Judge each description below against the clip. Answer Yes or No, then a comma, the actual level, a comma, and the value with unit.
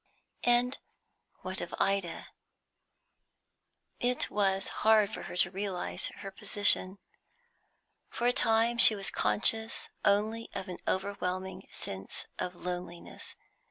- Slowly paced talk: Yes, slow, 115 wpm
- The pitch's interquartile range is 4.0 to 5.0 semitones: No, average, 3.0 semitones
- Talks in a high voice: Yes, high, 200 Hz